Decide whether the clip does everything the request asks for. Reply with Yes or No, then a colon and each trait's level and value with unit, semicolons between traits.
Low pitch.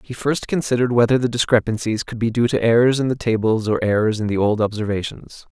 Yes: low, 115 Hz